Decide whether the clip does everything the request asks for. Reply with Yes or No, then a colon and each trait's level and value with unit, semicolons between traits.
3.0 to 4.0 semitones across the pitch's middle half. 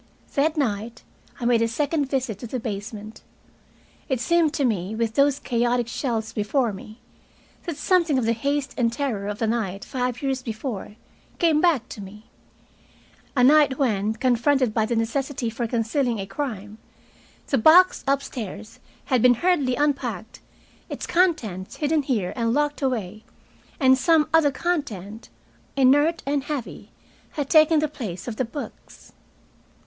No: average, 4.6 semitones